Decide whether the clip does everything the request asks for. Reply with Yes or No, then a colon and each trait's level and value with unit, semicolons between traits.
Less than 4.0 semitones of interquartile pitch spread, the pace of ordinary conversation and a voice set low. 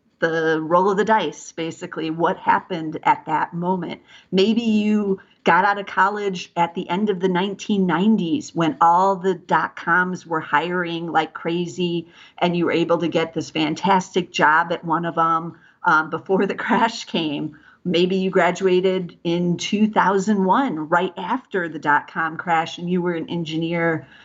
No: narrow, 2.6 semitones; average, 165 wpm; medium, 175 Hz